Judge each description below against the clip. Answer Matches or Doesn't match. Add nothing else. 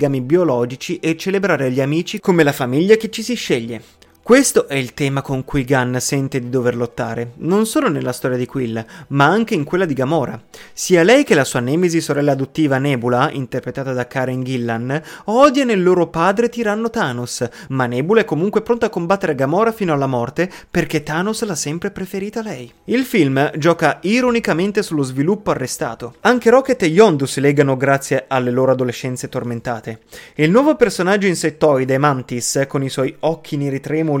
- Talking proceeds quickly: Matches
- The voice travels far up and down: Matches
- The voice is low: Doesn't match